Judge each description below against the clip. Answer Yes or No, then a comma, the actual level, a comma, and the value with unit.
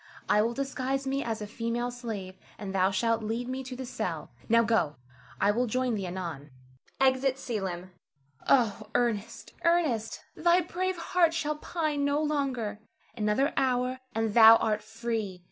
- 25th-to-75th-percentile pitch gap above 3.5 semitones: Yes, average, 4.1 semitones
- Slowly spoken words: No, average, 160 wpm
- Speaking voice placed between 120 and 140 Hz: No, high, 235 Hz